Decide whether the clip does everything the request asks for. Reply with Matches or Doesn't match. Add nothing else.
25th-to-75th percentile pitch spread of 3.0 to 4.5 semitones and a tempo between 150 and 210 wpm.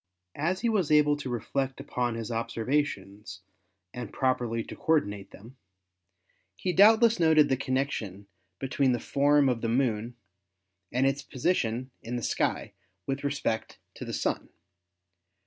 Doesn't match